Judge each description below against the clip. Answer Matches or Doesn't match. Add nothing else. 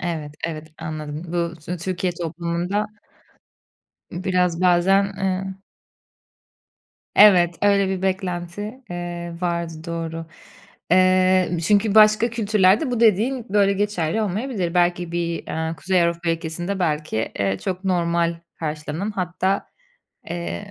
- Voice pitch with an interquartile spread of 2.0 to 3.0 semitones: Matches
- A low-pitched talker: Doesn't match